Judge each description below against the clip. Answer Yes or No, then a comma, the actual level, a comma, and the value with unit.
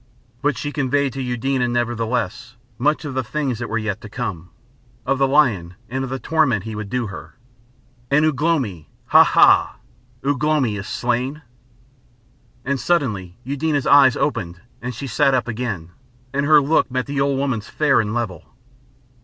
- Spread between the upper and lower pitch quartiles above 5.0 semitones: No, average, 4.0 semitones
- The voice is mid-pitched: No, low, 125 Hz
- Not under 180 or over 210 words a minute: No, average, 170 wpm